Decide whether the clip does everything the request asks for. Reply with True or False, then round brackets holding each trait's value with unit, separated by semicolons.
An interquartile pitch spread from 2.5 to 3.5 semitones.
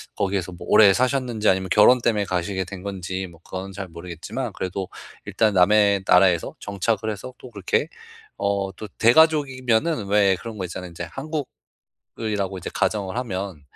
True (3.1 semitones)